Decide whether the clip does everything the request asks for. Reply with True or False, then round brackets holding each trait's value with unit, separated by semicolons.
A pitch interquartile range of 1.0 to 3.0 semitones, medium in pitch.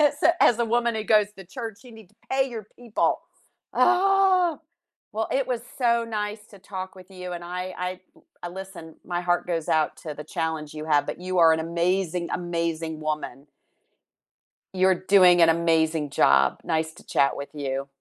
False (5.2 semitones; 180 Hz)